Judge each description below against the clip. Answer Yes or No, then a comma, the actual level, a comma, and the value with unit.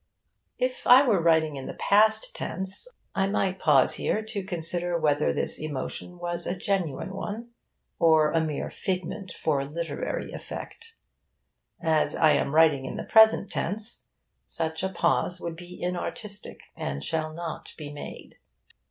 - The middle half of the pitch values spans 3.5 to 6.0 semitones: Yes, average, 4.1 semitones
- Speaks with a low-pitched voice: No, medium, 175 Hz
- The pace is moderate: Yes, average, 150 wpm